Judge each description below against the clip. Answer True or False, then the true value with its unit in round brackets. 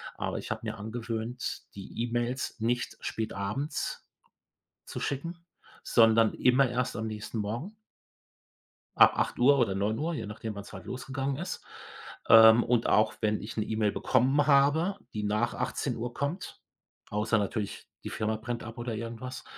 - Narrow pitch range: False (3.2 semitones)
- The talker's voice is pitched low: True (115 Hz)